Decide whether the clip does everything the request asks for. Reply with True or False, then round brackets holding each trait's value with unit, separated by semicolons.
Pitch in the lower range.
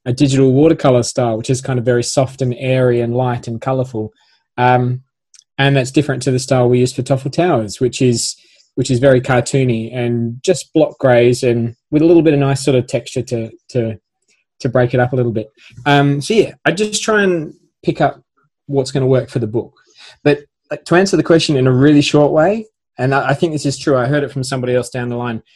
True (130 Hz)